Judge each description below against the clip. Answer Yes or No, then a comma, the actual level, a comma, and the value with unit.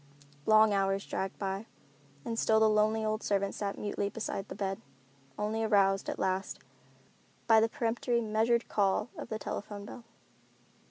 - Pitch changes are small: Yes, narrow, 2.0 semitones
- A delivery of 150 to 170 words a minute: Yes, average, 155 wpm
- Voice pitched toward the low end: No, high, 215 Hz